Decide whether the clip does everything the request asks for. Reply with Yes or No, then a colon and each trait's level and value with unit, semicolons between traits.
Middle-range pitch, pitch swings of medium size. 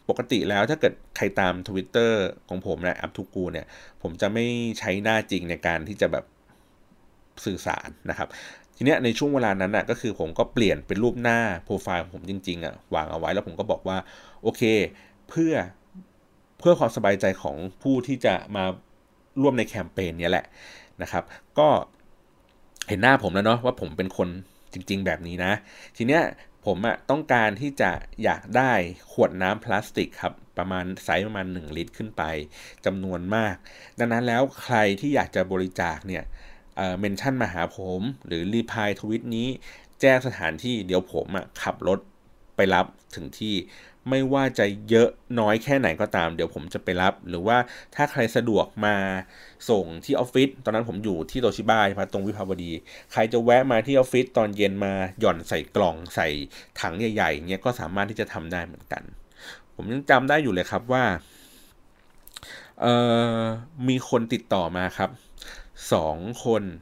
No: low, 105 Hz; average, 4.4 semitones